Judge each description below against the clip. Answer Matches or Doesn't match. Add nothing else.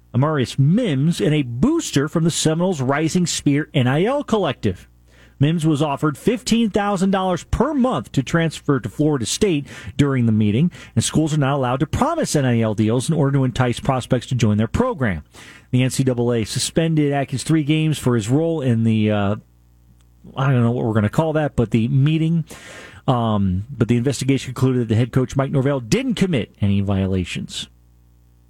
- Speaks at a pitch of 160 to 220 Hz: Doesn't match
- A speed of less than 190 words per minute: Matches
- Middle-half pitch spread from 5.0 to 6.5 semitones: Matches